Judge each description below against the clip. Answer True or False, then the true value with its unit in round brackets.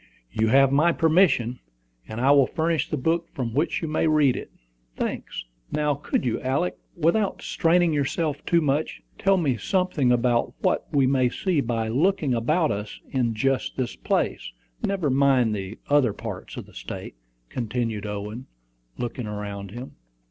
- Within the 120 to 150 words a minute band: False (165 wpm)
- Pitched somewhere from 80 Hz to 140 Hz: True (135 Hz)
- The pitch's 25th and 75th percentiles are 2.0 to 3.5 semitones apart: False (5.1 semitones)